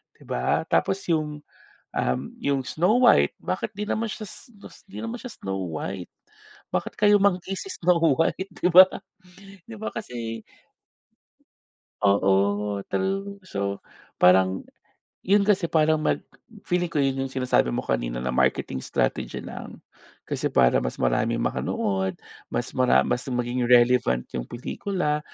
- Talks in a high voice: No, low, 135 Hz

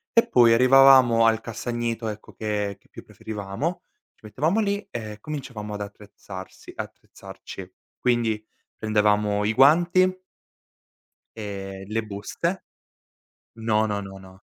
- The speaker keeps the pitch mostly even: No, average, 3.8 semitones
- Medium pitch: No, low, 110 Hz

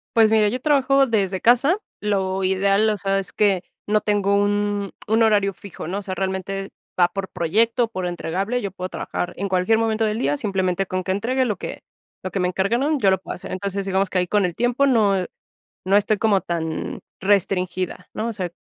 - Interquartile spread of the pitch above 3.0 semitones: No, average, 2.7 semitones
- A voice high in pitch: Yes, high, 200 Hz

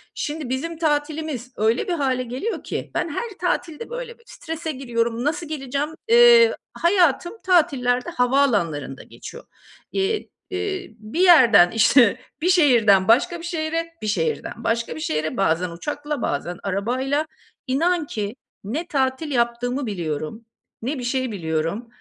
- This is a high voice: Yes, very high, 265 Hz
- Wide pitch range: Yes, wide, 6.6 semitones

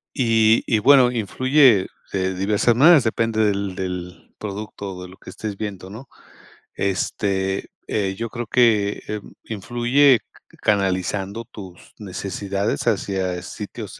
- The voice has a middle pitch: No, low, 105 Hz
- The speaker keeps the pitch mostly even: No, average, 3.3 semitones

